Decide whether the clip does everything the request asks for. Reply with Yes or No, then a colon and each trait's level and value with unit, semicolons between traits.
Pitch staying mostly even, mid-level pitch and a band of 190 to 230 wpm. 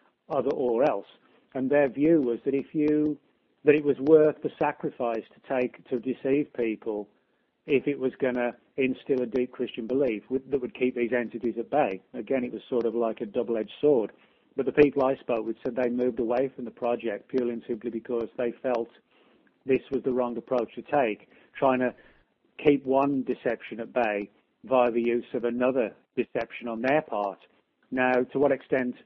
No: narrow, 2.3 semitones; low, 125 Hz; average, 195 wpm